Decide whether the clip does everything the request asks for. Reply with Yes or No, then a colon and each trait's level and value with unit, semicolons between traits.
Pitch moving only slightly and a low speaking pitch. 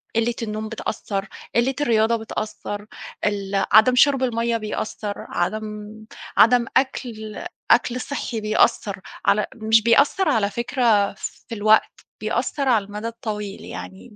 No: narrow, 2.1 semitones; high, 220 Hz